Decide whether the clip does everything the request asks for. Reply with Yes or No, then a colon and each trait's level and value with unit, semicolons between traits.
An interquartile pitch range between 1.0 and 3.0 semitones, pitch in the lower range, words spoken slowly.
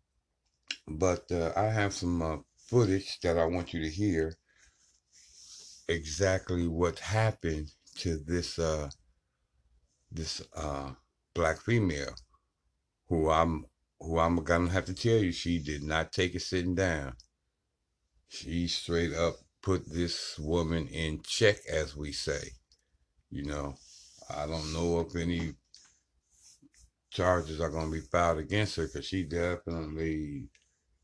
Yes: narrow, 2.5 semitones; very low, 80 Hz; slow, 130 wpm